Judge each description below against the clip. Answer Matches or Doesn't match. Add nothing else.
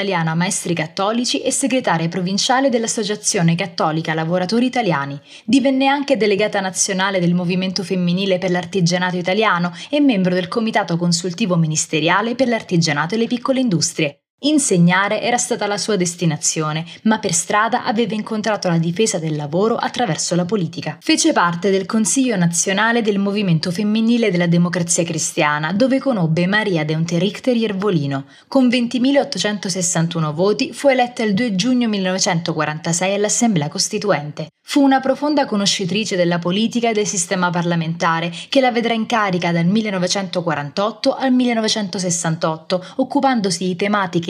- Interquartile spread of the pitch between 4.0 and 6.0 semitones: Matches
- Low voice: Doesn't match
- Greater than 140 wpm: Doesn't match